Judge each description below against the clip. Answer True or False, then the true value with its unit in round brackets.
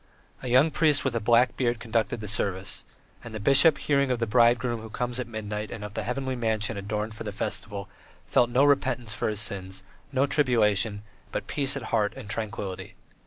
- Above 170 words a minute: True (200 wpm)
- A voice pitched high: False (115 Hz)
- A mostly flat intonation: False (3.2 semitones)